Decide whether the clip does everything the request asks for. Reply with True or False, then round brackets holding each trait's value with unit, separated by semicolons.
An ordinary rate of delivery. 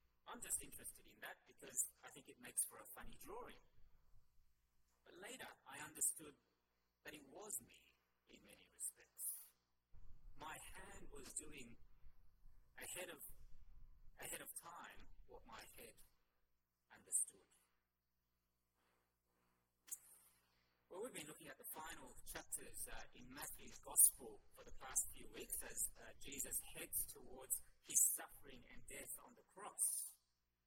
False (130 wpm)